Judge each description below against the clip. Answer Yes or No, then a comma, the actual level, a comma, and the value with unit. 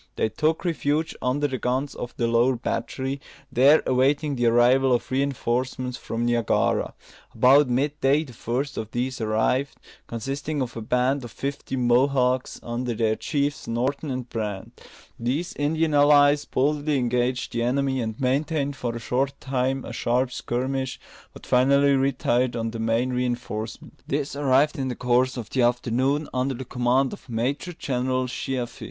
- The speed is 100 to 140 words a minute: No, average, 160 wpm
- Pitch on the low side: Yes, low, 130 Hz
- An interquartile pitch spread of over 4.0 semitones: No, narrow, 2.5 semitones